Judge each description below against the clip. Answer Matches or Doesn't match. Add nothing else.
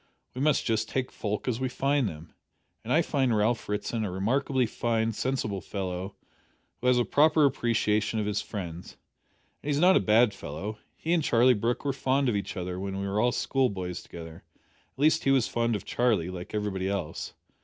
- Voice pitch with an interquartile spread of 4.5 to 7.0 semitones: Matches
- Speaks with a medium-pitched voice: Doesn't match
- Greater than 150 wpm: Matches